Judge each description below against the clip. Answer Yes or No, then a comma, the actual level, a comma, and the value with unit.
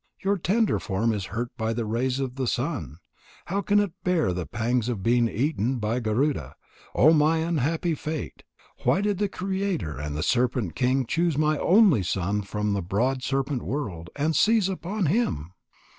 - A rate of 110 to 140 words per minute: No, average, 175 wpm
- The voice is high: No, low, 130 Hz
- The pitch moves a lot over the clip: Yes, wide, 7.6 semitones